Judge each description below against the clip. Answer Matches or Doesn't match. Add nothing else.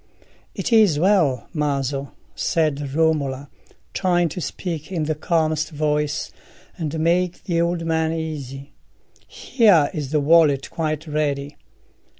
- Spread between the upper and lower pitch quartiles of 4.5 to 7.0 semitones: Doesn't match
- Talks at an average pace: Doesn't match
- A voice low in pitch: Doesn't match